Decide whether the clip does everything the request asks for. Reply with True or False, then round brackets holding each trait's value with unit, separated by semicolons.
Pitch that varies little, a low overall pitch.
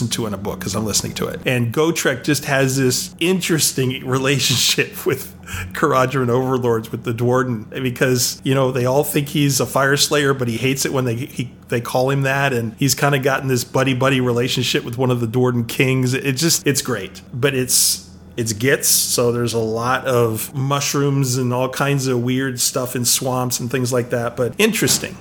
True (2.3 semitones; 130 Hz)